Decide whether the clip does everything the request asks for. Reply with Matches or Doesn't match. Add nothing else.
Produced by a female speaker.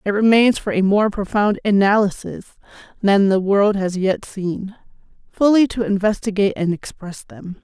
Matches